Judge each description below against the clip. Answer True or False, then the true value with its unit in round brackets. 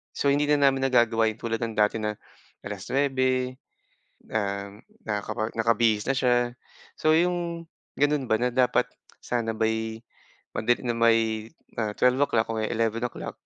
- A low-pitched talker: True (115 Hz)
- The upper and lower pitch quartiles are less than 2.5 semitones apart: False (2.8 semitones)